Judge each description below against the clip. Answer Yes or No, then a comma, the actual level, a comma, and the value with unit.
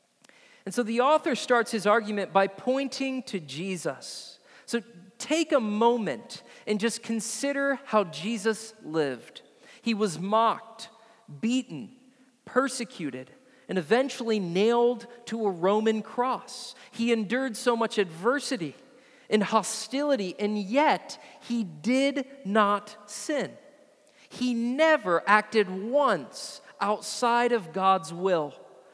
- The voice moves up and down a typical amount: Yes, average, 3.7 semitones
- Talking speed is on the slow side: Yes, slow, 110 wpm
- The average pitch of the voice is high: Yes, high, 230 Hz